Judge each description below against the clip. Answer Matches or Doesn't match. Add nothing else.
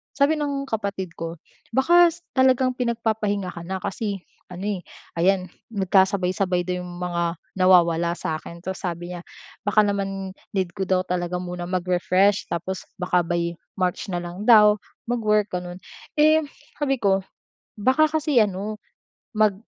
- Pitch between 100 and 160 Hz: Doesn't match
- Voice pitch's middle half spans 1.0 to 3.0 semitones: Doesn't match